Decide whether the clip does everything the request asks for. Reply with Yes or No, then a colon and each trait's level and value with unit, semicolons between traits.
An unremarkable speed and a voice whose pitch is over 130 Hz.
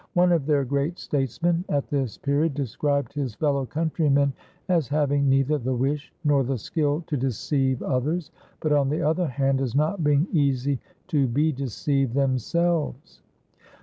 Yes: average, 155 wpm; medium, 140 Hz